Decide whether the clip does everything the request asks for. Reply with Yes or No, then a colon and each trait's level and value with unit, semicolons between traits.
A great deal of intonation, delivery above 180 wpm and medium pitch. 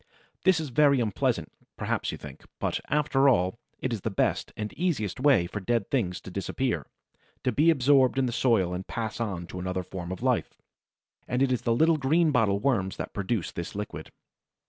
No: wide, 6.1 semitones; average, 190 wpm; low, 115 Hz